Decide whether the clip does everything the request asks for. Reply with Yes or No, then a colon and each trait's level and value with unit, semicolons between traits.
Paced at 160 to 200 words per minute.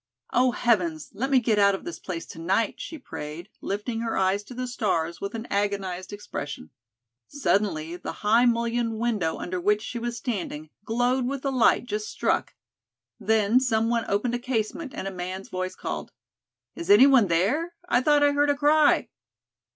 Yes: average, 175 wpm